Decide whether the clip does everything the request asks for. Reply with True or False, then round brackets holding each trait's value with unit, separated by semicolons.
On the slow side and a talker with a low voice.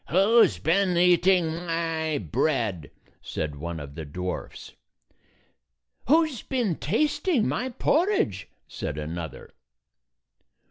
False (110 wpm; 165 Hz)